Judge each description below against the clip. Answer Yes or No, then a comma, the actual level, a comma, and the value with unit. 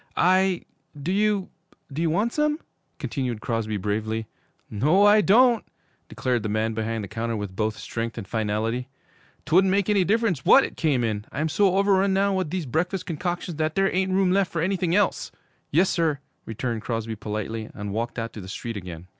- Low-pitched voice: No, medium, 150 Hz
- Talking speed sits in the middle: Yes, average, 190 wpm